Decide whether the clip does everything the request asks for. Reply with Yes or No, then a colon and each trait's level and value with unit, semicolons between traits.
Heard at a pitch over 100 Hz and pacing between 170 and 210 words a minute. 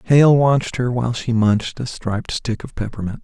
Yes: low, 120 Hz; fast, 205 wpm